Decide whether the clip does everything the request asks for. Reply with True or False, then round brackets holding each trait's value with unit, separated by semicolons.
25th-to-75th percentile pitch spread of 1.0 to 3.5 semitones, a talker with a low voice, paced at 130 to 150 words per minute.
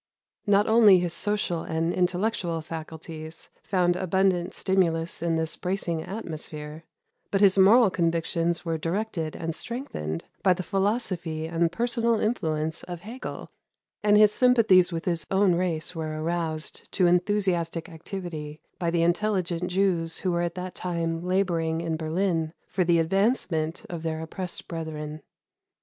False (2.9 semitones; 175 Hz; 140 wpm)